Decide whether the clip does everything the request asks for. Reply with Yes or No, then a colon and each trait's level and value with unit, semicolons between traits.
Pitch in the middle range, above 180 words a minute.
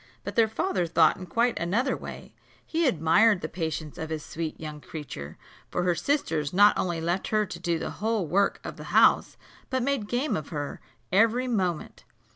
Yes: medium, 180 Hz; average, 190 wpm